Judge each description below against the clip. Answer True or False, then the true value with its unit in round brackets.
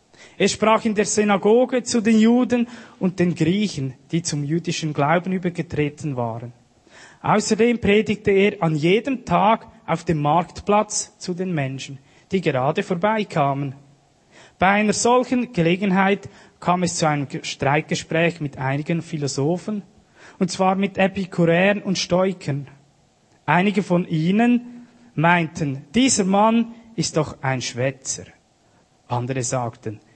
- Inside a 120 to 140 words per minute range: True (125 wpm)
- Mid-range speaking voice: True (175 Hz)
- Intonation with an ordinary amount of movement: False (6.4 semitones)